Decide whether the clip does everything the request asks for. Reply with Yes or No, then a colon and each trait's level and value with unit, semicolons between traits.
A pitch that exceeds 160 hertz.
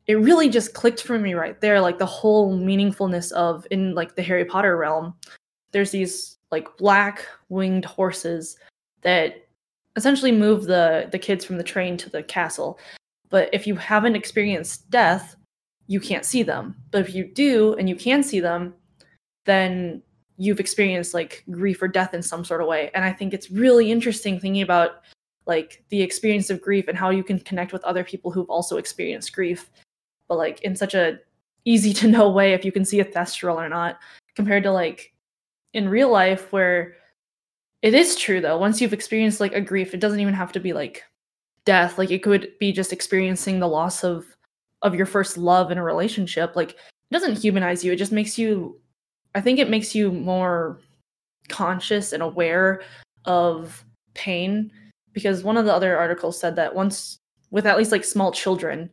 Yes: high, 190 Hz